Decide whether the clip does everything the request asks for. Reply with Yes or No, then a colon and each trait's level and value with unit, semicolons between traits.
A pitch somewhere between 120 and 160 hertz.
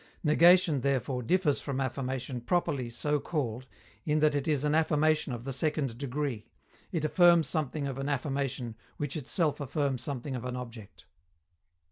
Yes: medium, 140 Hz